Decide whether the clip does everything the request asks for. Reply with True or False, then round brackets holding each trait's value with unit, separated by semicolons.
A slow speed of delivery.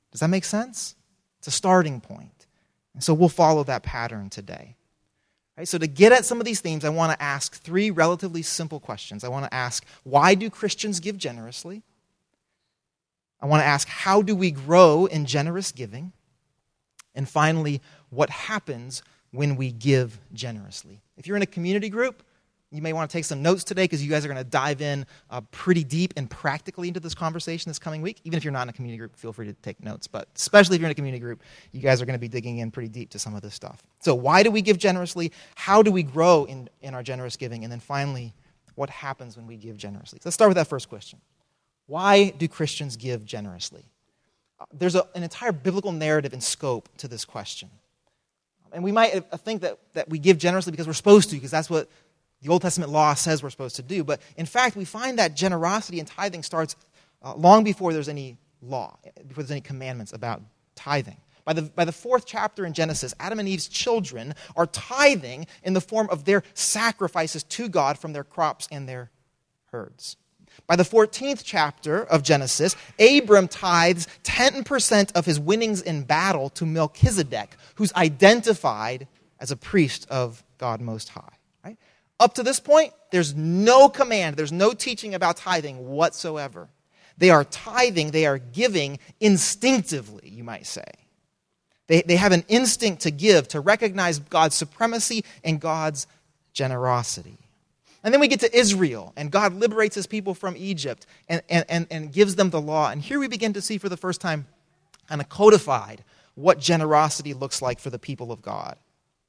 False (195 wpm)